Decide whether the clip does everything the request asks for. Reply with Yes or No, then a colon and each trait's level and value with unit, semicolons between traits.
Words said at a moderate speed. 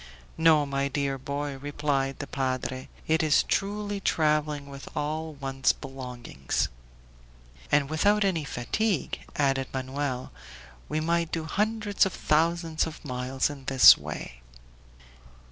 No: slow, 125 wpm